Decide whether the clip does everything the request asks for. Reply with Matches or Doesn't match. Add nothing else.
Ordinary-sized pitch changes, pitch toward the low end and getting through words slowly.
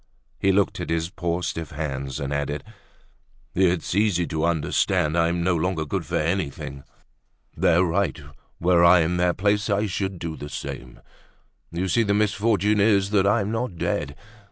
Doesn't match